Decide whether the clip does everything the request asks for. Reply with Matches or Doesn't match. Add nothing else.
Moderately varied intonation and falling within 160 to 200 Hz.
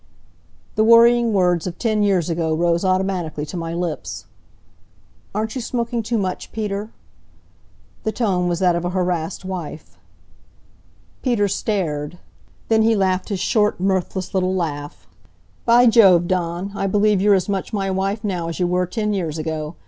Matches